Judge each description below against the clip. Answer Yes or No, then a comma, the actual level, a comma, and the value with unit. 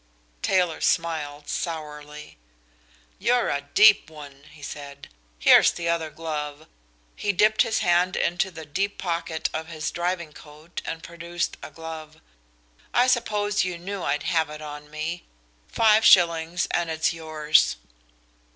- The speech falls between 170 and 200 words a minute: No, average, 140 wpm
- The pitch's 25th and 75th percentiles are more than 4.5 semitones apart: No, average, 2.7 semitones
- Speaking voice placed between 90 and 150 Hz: No, medium, 165 Hz